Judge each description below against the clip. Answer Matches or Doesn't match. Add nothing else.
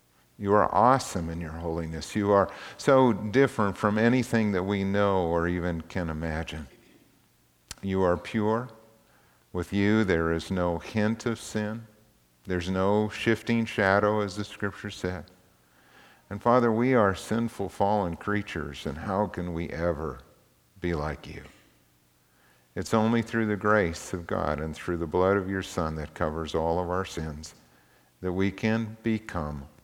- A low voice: Matches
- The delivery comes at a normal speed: Matches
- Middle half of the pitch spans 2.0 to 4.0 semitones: Doesn't match